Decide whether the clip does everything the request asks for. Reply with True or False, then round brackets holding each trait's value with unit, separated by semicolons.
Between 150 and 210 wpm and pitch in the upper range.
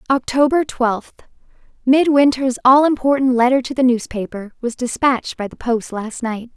False (135 wpm; 250 Hz)